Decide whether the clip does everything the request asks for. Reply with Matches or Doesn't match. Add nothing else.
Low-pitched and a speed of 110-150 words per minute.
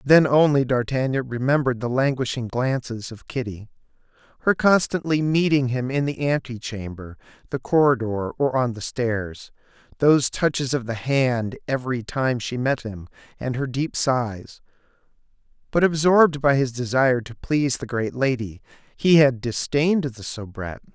Matches